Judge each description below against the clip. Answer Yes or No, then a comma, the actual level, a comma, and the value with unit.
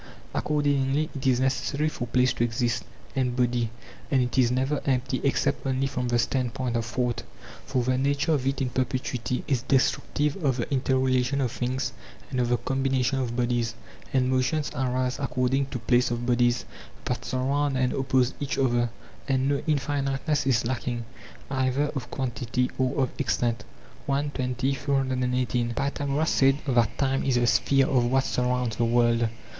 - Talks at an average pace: Yes, average, 165 wpm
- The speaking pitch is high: No, low, 130 Hz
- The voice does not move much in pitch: Yes, narrow, 1.8 semitones